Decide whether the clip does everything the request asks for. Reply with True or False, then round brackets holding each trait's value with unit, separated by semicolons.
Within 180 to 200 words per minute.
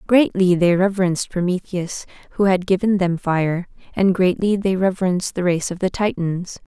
False (160 wpm)